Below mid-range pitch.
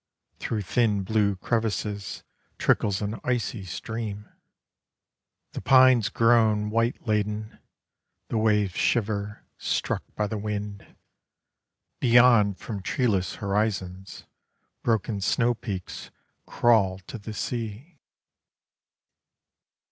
Yes: low, 105 Hz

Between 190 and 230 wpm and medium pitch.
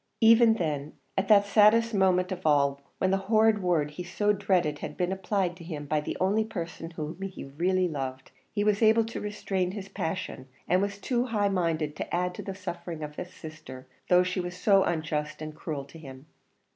Yes: fast, 205 wpm; medium, 180 Hz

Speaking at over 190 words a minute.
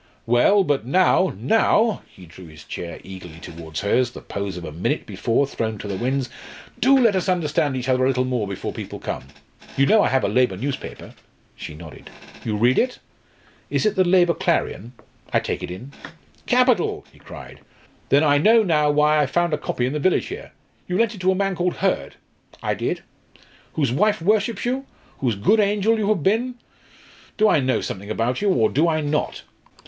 Yes: average, 200 wpm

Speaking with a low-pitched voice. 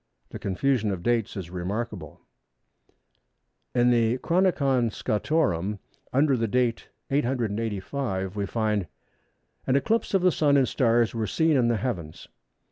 Yes: low, 120 Hz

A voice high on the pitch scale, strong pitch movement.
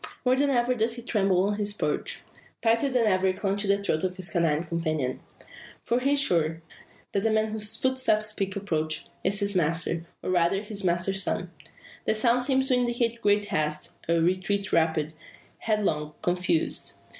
No: high, 200 Hz; average, 4.7 semitones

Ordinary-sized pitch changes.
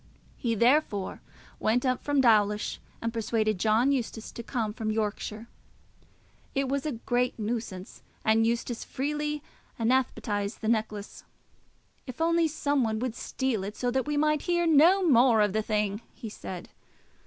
Yes: average, 4.1 semitones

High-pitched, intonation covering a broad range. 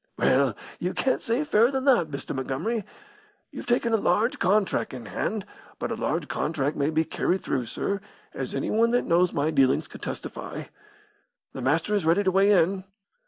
No: medium, 180 Hz; wide, 6.8 semitones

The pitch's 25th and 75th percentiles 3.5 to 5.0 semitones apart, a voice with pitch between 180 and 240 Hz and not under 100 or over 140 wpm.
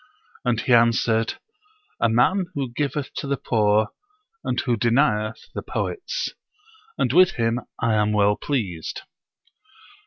No: average, 4.2 semitones; low, 120 Hz; slow, 135 wpm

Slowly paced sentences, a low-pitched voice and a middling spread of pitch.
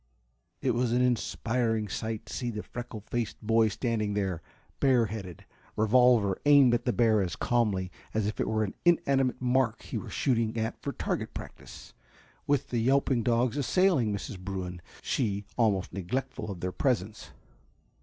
No: average, 165 wpm; low, 115 Hz; average, 3.3 semitones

